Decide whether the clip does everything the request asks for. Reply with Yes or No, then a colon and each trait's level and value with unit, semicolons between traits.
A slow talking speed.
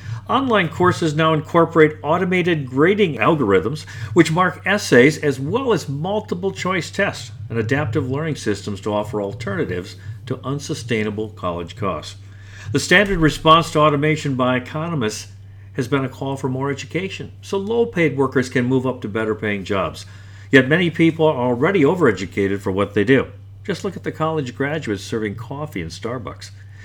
No: average, 160 wpm